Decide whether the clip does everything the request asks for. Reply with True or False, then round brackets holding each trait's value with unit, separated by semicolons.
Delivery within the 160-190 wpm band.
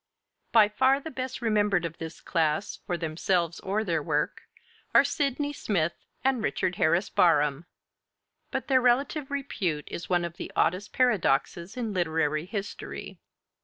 False (150 wpm)